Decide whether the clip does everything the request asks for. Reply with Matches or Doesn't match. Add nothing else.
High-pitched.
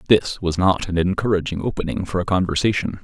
Doesn't match